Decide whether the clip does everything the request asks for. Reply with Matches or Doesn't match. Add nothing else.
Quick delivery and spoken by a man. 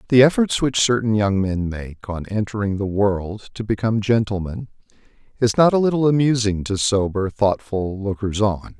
Doesn't match